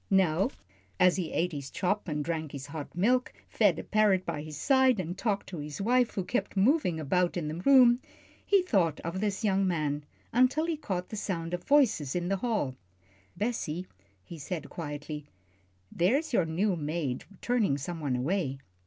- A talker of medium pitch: Yes, medium, 180 Hz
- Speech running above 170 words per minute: Yes, average, 180 wpm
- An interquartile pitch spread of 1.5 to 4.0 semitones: No, wide, 5.6 semitones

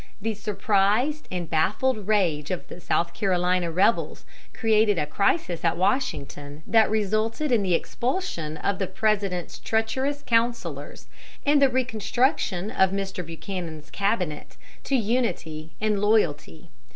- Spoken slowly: Yes, slow, 125 wpm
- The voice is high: Yes, high, 200 Hz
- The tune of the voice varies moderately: Yes, average, 4.6 semitones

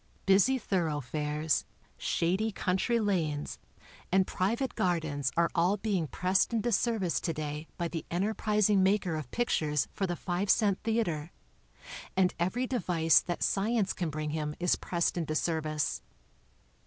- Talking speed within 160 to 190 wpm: No, average, 140 wpm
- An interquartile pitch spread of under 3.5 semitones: No, average, 4.6 semitones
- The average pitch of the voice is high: No, medium, 180 Hz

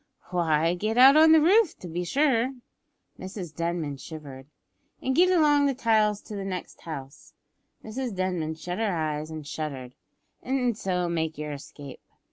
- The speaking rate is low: No, average, 160 wpm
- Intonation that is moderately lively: No, wide, 7.9 semitones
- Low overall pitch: No, medium, 180 Hz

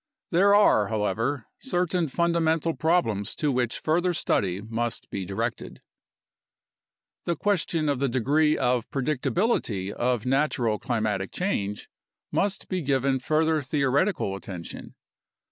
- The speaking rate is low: Yes, slow, 115 wpm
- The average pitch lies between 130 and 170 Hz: Yes, low, 135 Hz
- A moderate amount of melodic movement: No, wide, 6.8 semitones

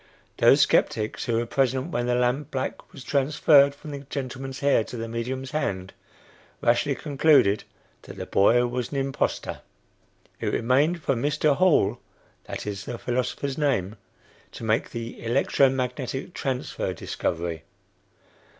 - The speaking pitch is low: Yes, low, 130 Hz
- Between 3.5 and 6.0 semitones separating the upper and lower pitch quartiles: No, average, 3.1 semitones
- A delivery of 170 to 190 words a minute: No, average, 140 wpm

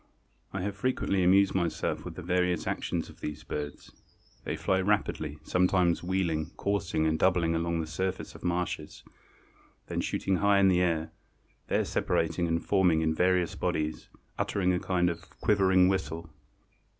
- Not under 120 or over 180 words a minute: Yes, average, 160 wpm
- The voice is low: Yes, very low, 90 Hz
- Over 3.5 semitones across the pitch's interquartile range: No, narrow, 2.5 semitones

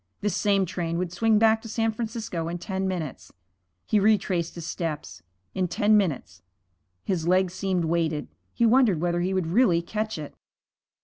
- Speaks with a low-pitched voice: No, medium, 185 Hz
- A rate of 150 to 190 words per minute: Yes, average, 170 wpm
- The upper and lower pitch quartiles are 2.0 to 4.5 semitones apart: Yes, average, 4.0 semitones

